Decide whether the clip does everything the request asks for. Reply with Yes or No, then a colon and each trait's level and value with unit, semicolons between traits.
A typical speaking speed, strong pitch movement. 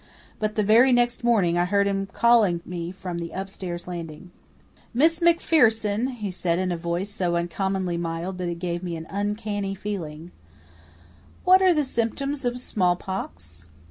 No: average, 160 wpm; average, 4.7 semitones